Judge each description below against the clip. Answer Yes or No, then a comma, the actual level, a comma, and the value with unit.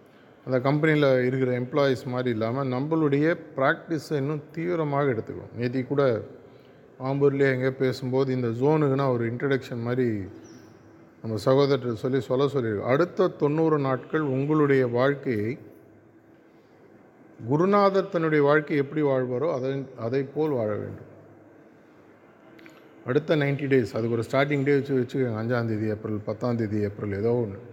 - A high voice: No, low, 135 Hz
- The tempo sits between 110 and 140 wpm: Yes, average, 125 wpm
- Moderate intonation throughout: Yes, average, 3.0 semitones